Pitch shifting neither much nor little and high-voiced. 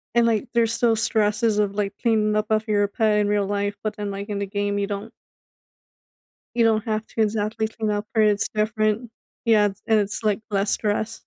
No: narrow, 1.3 semitones; high, 215 Hz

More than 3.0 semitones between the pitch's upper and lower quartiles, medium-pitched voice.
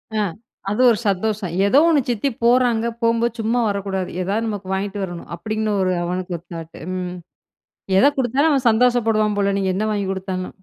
No: average, 3.4 semitones; high, 210 Hz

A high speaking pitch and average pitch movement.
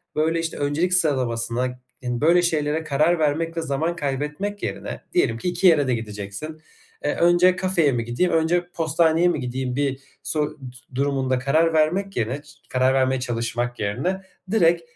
No: medium, 150 Hz; average, 4.6 semitones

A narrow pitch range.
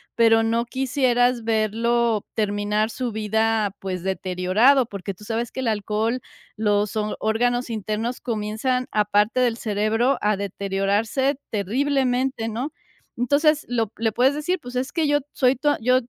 No: average, 3.2 semitones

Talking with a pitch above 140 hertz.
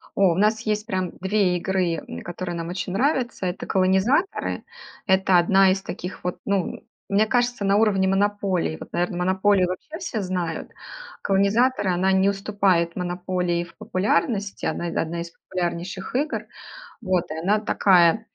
Yes: high, 190 Hz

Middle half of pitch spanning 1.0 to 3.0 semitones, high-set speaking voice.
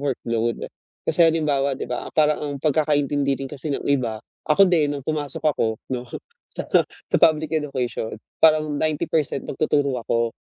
No: narrow, 2.6 semitones; medium, 145 Hz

